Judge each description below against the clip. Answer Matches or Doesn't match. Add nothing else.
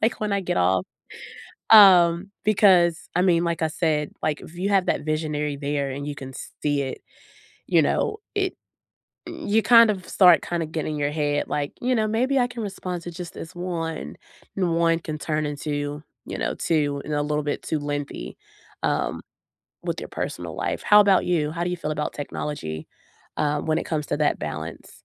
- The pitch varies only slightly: Doesn't match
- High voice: Doesn't match